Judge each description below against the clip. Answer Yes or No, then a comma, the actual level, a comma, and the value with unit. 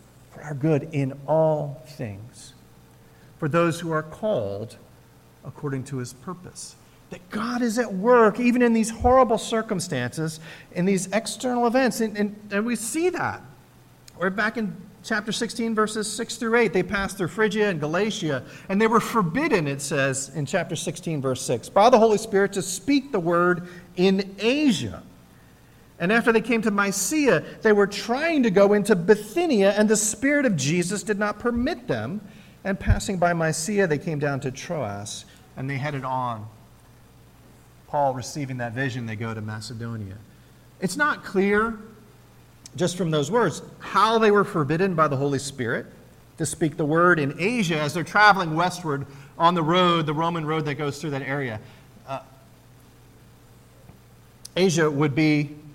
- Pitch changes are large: Yes, wide, 7.2 semitones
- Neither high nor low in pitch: Yes, medium, 175 Hz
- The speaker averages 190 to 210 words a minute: No, average, 165 wpm